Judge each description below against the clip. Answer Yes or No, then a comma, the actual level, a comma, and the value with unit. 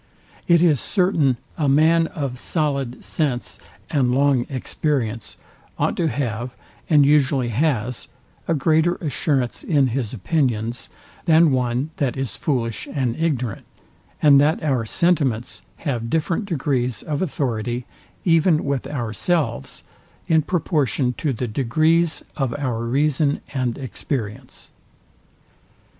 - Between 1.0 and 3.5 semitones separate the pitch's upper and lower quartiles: No, average, 4.1 semitones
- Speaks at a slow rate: Yes, slow, 120 wpm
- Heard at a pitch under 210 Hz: Yes, medium, 140 Hz